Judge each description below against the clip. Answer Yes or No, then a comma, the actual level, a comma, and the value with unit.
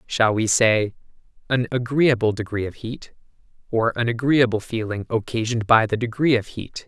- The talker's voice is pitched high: No, low, 115 Hz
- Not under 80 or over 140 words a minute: No, average, 155 wpm